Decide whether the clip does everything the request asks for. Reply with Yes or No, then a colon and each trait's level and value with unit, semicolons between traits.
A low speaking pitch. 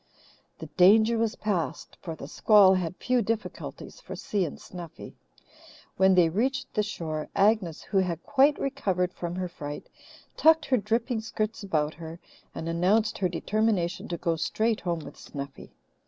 No: high, 190 Hz